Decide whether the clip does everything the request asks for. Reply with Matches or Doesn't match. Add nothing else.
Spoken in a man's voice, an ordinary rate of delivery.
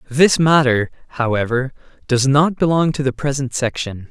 Matches